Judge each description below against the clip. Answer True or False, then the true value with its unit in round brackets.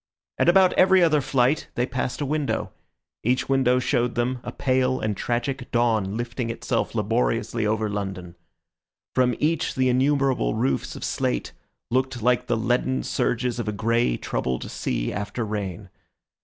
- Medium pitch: False (120 Hz)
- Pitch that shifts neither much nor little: True (3.5 semitones)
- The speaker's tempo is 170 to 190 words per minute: False (155 wpm)